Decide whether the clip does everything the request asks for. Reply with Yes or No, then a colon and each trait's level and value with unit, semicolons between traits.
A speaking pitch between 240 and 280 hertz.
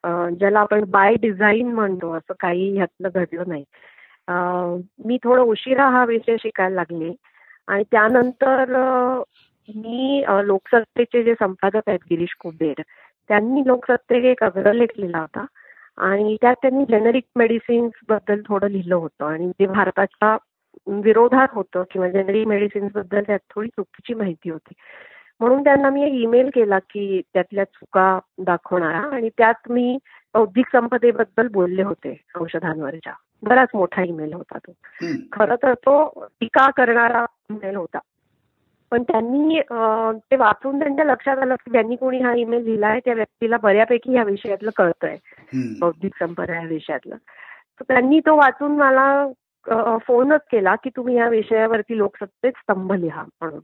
No: high, 220 Hz